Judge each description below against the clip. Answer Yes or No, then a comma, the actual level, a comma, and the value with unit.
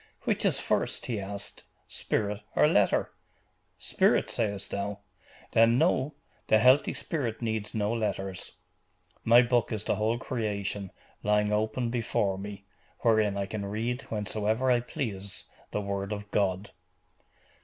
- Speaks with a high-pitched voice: No, low, 105 Hz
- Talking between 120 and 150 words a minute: Yes, slow, 135 wpm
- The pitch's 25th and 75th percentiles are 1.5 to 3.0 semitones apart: Yes, narrow, 2.4 semitones